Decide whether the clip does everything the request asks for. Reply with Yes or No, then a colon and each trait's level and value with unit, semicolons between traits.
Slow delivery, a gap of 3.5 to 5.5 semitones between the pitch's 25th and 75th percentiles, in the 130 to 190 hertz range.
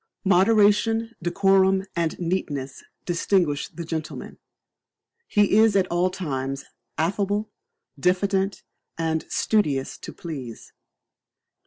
Yes: slow, 95 wpm; average, 3.9 semitones; medium, 185 Hz